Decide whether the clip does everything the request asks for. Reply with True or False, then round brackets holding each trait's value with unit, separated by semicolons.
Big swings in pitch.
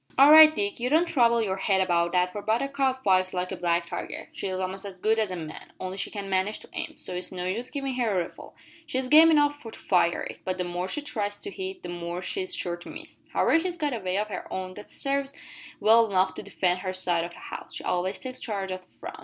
True (6.1 semitones)